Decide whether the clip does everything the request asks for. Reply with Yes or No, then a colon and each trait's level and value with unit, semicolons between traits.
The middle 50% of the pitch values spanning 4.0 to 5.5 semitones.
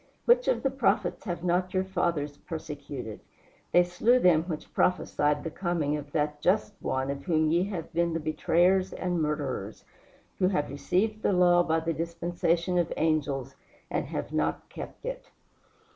No: average, 3.3 semitones